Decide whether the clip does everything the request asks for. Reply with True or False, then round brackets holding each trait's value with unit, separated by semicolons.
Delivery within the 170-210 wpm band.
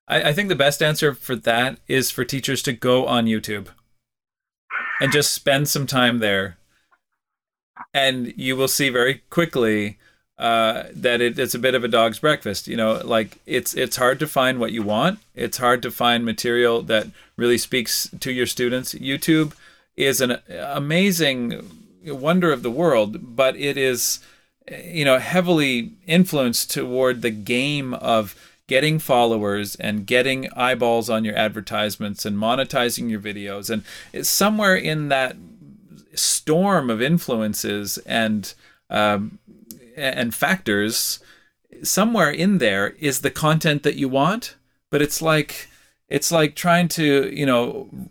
False (150 wpm)